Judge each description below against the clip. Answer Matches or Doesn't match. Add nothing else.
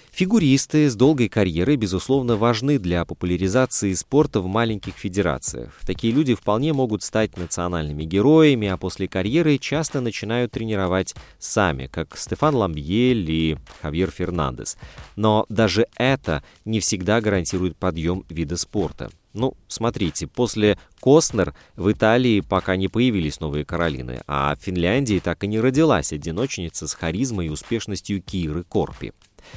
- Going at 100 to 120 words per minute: Doesn't match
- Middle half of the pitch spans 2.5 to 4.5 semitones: Doesn't match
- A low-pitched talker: Matches